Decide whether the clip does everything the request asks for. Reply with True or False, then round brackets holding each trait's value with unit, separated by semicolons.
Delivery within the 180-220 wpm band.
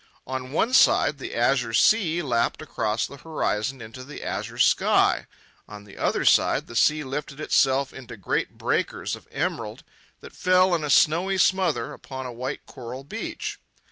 False (165 wpm)